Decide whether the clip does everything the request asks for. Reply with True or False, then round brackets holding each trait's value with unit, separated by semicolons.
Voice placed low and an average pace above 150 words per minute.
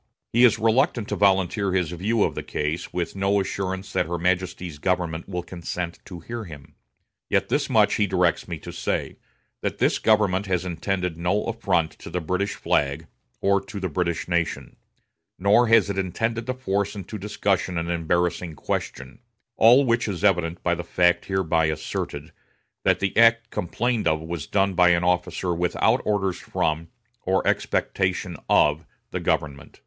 True (90 Hz; 170 wpm)